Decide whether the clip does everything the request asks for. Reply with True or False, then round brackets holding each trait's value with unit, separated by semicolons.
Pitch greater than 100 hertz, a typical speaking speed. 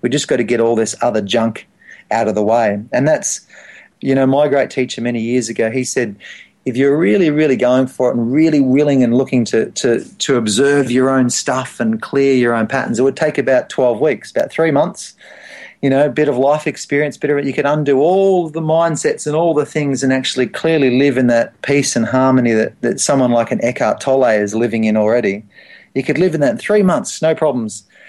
False (135 Hz; 230 wpm)